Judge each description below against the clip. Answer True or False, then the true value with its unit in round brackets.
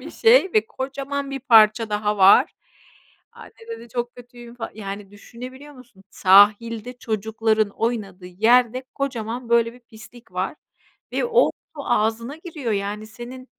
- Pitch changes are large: False (3.2 semitones)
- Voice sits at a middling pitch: False (235 Hz)